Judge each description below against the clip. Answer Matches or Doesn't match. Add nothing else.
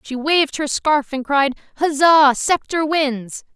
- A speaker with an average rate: Matches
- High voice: Matches